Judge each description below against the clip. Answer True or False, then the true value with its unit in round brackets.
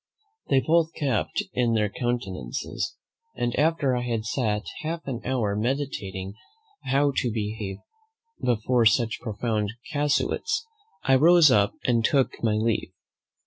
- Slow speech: True (125 wpm)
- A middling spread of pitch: True (4.3 semitones)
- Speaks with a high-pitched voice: False (120 Hz)